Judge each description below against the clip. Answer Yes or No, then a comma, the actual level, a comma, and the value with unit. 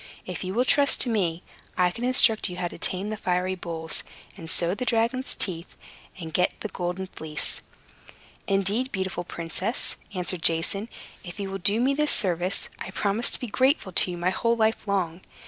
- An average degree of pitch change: Yes, average, 4.1 semitones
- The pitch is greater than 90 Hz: Yes, high, 190 Hz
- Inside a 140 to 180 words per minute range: No, average, 190 wpm